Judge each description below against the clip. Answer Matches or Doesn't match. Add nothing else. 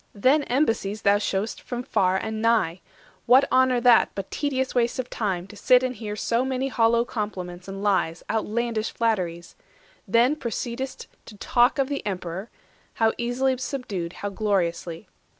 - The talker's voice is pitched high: Matches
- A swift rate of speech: Doesn't match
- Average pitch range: Matches